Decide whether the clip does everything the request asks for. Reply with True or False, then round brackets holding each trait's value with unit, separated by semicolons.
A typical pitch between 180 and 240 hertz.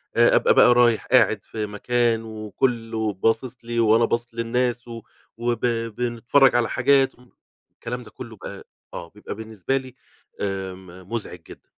False (115 Hz)